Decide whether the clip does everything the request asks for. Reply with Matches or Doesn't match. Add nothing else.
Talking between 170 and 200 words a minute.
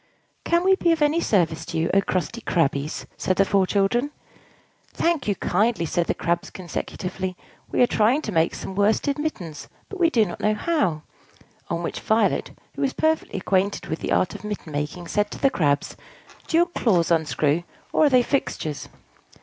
Matches